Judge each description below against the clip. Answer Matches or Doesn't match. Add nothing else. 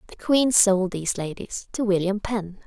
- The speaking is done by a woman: Matches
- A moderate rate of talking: Matches